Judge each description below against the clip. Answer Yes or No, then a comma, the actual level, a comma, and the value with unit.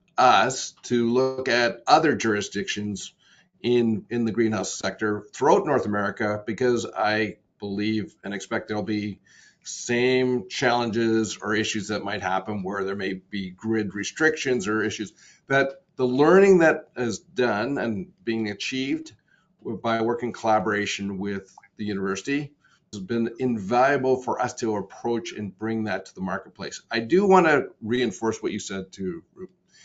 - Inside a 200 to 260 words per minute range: No, average, 150 wpm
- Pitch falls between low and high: No, low, 110 Hz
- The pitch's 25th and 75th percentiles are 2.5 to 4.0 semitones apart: Yes, average, 3.5 semitones